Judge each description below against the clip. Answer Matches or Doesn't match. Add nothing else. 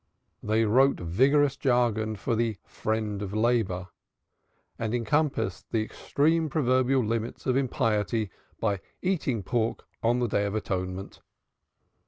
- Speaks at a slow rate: Matches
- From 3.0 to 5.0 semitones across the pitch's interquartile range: Matches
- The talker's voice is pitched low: Matches